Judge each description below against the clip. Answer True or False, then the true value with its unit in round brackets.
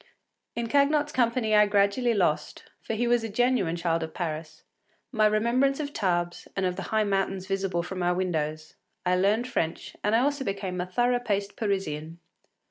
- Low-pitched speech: False (200 Hz)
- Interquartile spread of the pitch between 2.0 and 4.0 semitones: False (5.0 semitones)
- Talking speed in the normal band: True (180 wpm)